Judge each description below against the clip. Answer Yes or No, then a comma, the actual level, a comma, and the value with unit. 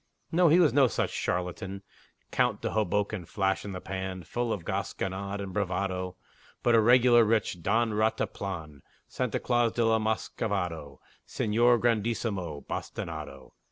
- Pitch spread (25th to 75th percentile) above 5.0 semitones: No, average, 3.8 semitones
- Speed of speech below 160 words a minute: Yes, average, 140 wpm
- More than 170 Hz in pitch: No, low, 105 Hz